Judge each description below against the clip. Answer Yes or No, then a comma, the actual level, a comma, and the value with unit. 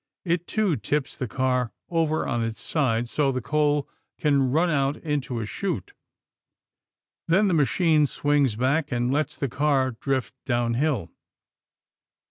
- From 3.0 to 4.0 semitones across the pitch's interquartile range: Yes, average, 3.6 semitones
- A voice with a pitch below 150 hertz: Yes, medium, 140 Hz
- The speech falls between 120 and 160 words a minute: Yes, average, 140 wpm